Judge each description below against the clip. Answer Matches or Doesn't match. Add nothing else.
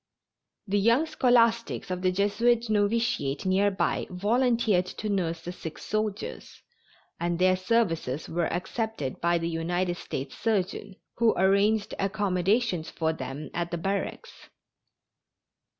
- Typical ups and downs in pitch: Matches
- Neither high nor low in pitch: Doesn't match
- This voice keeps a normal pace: Doesn't match